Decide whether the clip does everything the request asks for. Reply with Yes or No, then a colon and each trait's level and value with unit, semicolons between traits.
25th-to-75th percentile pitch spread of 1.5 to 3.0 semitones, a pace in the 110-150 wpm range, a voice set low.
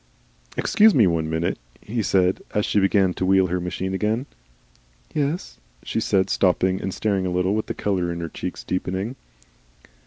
No: narrow, 2.6 semitones; average, 175 wpm; very low, 95 Hz